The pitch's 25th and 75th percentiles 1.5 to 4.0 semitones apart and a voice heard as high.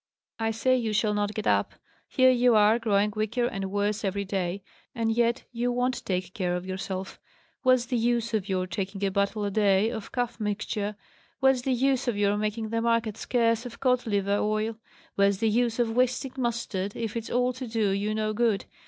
Yes: average, 3.0 semitones; high, 220 Hz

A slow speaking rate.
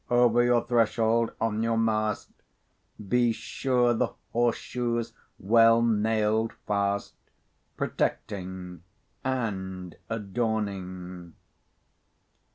Yes: slow, 80 wpm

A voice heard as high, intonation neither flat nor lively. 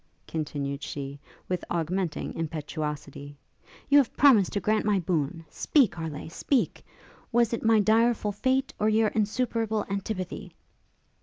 No: high, 200 Hz; wide, 6.0 semitones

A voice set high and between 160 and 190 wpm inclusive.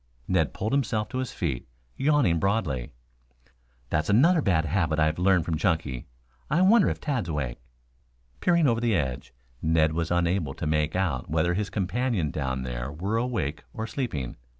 No: very low, 85 Hz; average, 170 wpm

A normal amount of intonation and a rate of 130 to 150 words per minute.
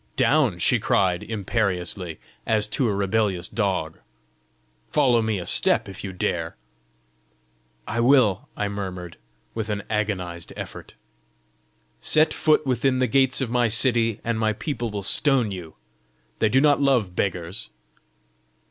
Yes: average, 4.4 semitones; average, 140 wpm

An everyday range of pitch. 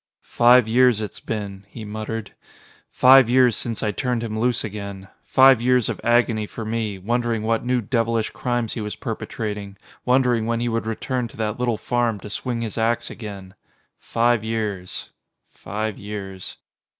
No: narrow, 2.3 semitones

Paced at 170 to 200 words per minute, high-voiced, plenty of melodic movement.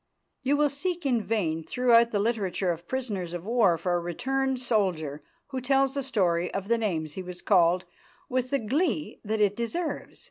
Yes: average, 185 wpm; high, 220 Hz; wide, 6.8 semitones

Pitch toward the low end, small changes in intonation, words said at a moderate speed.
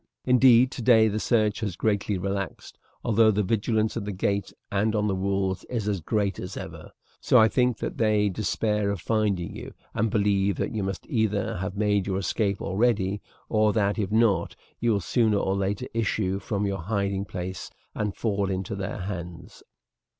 Yes: low, 100 Hz; narrow, 2.1 semitones; average, 180 wpm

